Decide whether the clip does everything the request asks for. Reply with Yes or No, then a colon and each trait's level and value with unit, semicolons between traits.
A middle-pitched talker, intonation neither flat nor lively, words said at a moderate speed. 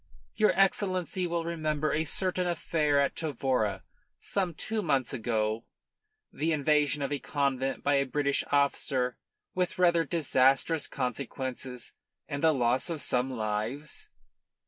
No: medium, 145 Hz; average, 4.1 semitones; slow, 130 wpm